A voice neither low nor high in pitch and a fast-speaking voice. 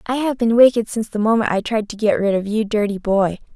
No: high, 215 Hz; fast, 270 wpm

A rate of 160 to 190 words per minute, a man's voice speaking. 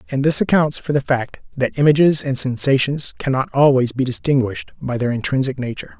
Yes: average, 180 wpm; male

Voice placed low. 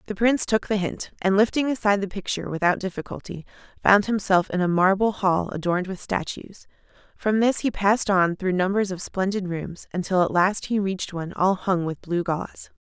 No: high, 190 Hz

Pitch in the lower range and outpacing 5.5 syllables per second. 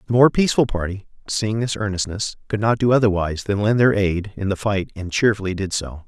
Yes: low, 105 Hz; 5.9 syllables/s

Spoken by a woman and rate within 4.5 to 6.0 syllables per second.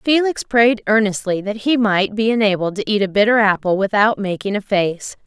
Yes: female; 5.1 syllables/s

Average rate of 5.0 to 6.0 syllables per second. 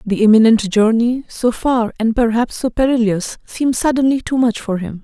Yes: 5.1 syllables/s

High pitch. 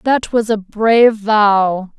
Yes: high, 215 Hz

